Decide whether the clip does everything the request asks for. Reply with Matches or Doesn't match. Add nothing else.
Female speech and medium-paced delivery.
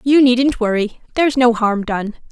Matches